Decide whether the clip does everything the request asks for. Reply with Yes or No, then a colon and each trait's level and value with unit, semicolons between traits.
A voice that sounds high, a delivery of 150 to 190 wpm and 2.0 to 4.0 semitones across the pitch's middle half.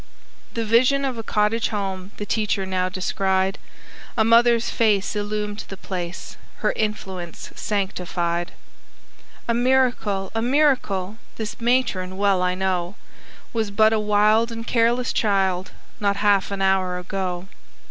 No: high, 205 Hz; slow, 135 wpm; average, 3.2 semitones